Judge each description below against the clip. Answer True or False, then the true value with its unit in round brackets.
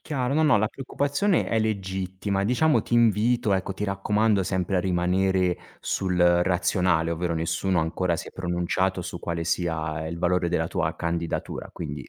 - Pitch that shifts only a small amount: False (3.2 semitones)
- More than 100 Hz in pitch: False (95 Hz)